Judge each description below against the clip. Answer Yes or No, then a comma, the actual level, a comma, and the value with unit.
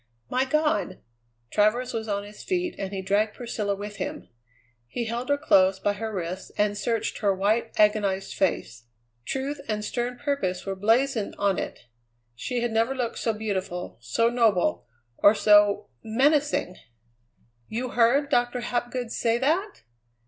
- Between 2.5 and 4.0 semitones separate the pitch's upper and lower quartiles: Yes, average, 3.7 semitones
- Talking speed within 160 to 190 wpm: No, average, 150 wpm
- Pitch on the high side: Yes, high, 220 Hz